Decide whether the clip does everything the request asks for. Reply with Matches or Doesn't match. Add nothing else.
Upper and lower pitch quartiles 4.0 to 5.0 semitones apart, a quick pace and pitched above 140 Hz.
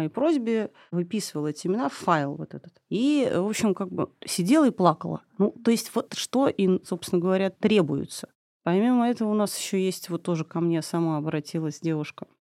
Matches